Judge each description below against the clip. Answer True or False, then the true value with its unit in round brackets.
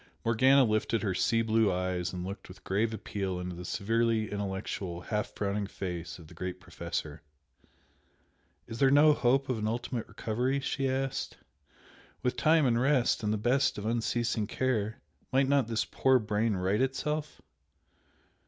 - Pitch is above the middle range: False (110 Hz)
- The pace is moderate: True (160 wpm)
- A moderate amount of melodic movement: True (4.8 semitones)